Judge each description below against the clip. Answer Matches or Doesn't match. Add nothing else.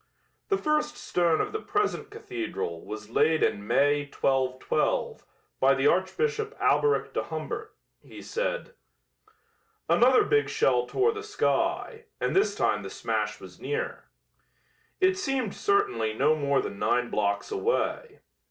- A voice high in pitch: Matches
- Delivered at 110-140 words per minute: Matches